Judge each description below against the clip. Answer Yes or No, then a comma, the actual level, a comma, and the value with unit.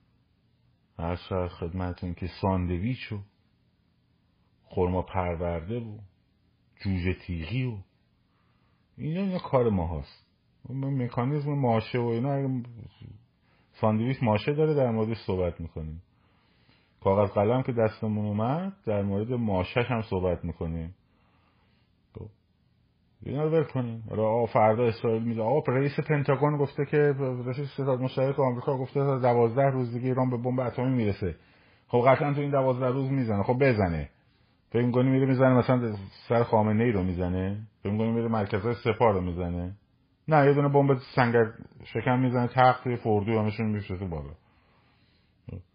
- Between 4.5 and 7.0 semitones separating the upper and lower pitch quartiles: Yes, average, 5.0 semitones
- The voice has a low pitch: Yes, low, 115 Hz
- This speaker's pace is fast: No, average, 130 wpm